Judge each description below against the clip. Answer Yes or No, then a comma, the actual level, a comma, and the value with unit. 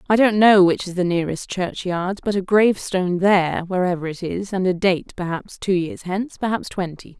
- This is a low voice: No, medium, 185 Hz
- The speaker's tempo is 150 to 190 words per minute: No, average, 200 wpm